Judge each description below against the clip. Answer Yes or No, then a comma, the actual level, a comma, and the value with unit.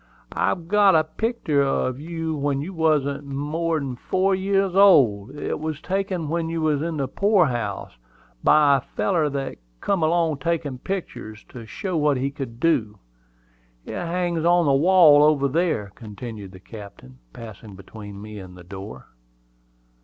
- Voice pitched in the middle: Yes, medium, 150 Hz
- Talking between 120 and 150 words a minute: No, average, 160 wpm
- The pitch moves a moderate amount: No, wide, 6.1 semitones